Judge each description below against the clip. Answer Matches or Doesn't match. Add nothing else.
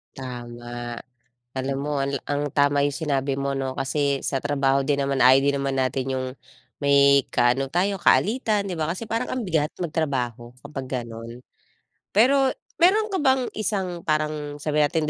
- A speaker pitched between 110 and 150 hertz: Matches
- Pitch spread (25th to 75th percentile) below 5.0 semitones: Matches